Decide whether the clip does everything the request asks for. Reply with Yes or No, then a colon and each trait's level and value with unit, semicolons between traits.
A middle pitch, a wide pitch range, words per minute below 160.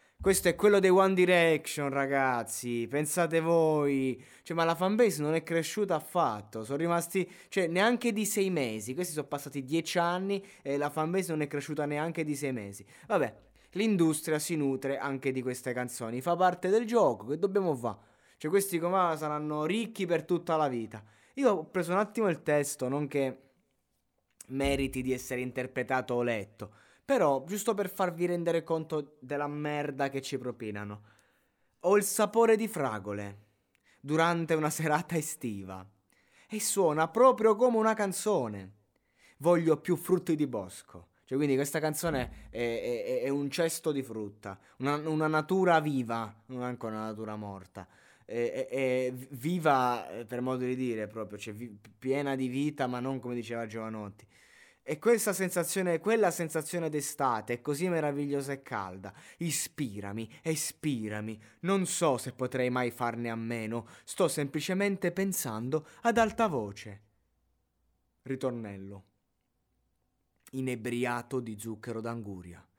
Yes: medium, 145 Hz; wide, 6.3 semitones; average, 150 wpm